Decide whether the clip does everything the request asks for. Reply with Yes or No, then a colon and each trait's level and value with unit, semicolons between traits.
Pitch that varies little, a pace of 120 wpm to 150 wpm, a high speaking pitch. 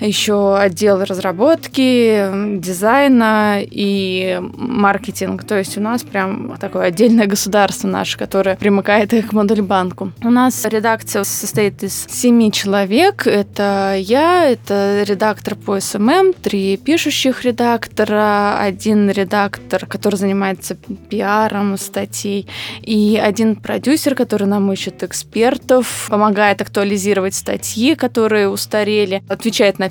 No: narrow, 2.2 semitones; slow, 110 wpm; high, 205 Hz